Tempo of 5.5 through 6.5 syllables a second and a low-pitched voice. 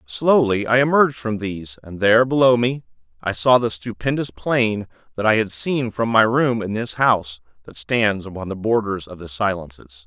No: 5.0 syllables/s; low, 110 Hz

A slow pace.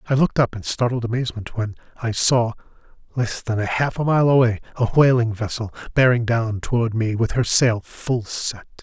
No: average, 185 wpm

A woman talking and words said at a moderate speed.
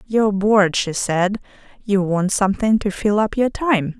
Yes: female; average, 180 wpm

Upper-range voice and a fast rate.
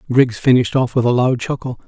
No: low, 125 Hz; fast, 225 wpm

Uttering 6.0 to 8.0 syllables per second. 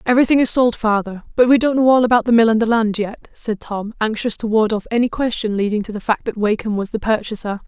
Yes: 6.2 syllables/s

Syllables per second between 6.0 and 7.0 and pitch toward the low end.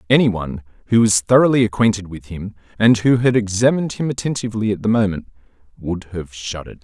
Yes: 6.4 syllables/s; low, 105 Hz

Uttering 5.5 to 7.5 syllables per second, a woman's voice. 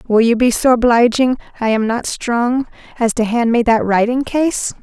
No: 4.7 syllables/s; female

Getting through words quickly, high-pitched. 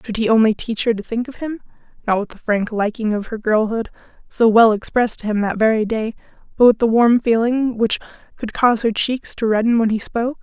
Yes: fast, 230 wpm; high, 225 Hz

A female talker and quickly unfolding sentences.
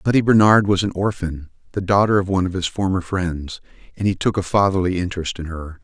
No: male; fast, 215 wpm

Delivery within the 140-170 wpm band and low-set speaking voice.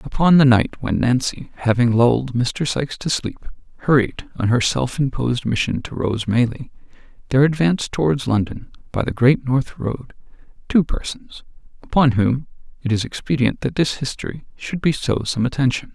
Yes: average, 160 wpm; low, 130 Hz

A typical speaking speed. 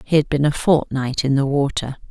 No: fast, 230 wpm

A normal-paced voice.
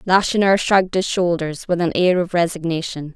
Yes: average, 170 wpm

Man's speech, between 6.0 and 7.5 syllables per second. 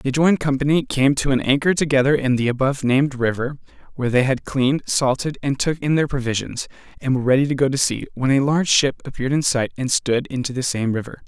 Yes: male; 6.3 syllables/s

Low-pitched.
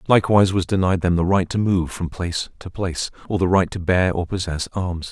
Yes: very low, 90 Hz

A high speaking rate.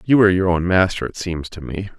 Yes: fast, 270 wpm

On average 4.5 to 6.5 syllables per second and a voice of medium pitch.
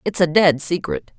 Yes: 4.7 syllables/s; medium, 175 Hz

